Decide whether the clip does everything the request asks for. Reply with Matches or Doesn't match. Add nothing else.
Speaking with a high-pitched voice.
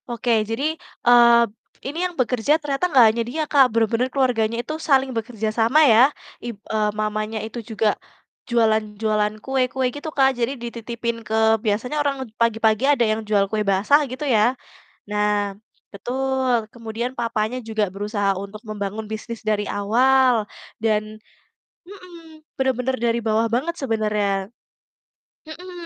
Matches